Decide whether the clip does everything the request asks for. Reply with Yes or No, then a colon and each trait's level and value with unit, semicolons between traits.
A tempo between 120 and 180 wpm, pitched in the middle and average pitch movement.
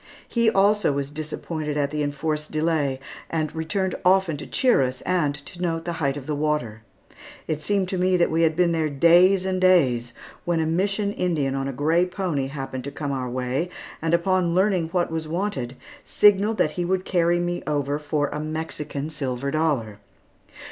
No: average, 190 wpm; medium, 160 Hz; average, 4.0 semitones